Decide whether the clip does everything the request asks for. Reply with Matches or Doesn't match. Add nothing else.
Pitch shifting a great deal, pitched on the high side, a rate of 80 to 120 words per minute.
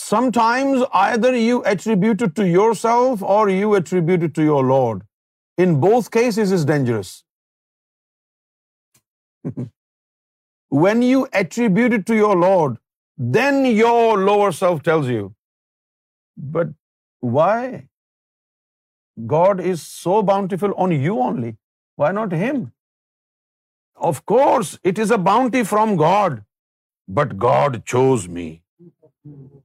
Matches